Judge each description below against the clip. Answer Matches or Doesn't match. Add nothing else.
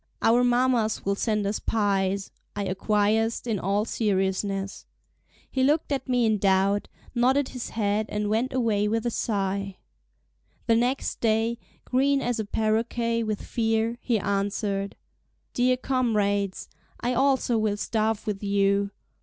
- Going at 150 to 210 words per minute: Doesn't match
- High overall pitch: Matches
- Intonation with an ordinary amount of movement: Matches